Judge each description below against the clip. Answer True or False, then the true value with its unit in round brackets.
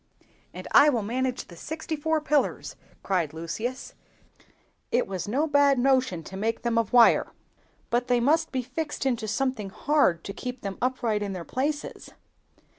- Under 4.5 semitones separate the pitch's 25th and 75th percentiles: False (5.0 semitones)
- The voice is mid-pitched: False (245 Hz)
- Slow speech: False (165 wpm)